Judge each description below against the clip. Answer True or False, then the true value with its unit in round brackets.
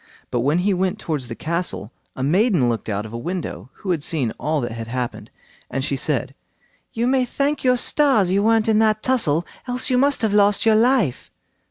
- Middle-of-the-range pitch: True (180 Hz)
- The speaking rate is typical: False (210 wpm)